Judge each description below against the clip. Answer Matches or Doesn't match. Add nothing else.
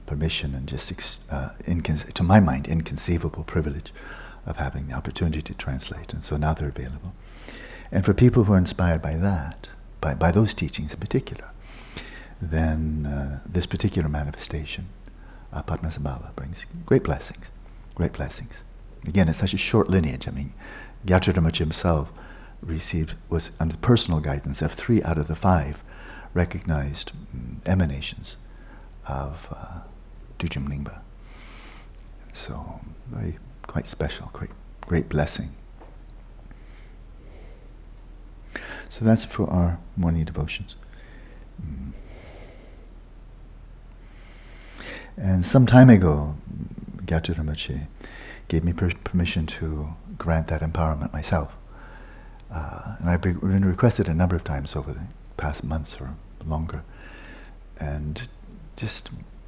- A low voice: Matches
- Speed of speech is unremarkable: Doesn't match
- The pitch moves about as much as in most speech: Matches